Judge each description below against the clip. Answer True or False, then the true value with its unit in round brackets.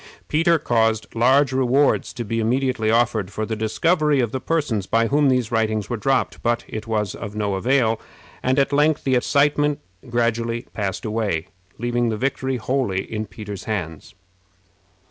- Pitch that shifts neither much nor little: True (3.6 semitones)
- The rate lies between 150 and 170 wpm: True (165 wpm)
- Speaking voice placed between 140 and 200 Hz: False (115 Hz)